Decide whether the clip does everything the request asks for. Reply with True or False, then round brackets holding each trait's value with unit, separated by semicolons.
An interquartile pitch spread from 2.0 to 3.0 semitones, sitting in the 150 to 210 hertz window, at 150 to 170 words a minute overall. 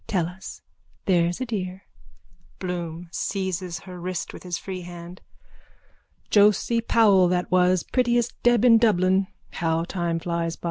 False (2.7 semitones; 185 Hz; 140 wpm)